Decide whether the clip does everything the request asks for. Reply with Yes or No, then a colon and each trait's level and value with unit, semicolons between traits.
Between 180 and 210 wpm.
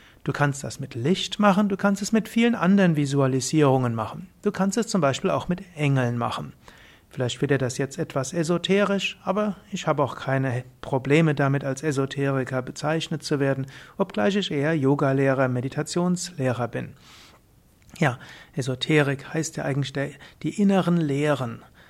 No: average, 155 wpm